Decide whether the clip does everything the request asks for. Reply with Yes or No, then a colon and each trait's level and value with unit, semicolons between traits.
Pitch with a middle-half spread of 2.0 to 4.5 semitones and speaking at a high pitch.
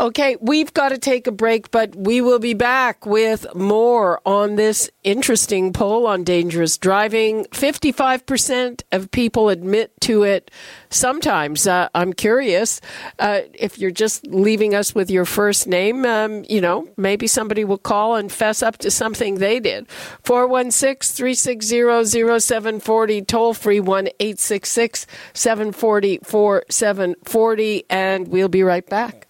Yes: average, 3.1 semitones; high, 215 Hz